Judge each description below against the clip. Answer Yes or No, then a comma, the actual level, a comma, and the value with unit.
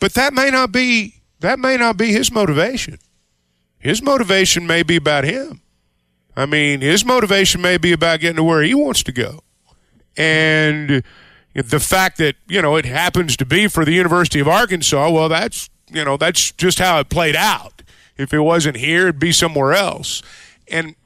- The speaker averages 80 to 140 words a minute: No, average, 185 wpm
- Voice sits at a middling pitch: Yes, medium, 165 Hz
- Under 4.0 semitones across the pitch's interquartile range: No, average, 4.5 semitones